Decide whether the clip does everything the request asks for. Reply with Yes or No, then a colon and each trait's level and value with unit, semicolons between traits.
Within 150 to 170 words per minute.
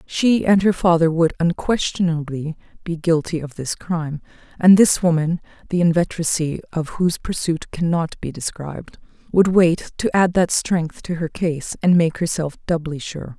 Yes: average, 160 wpm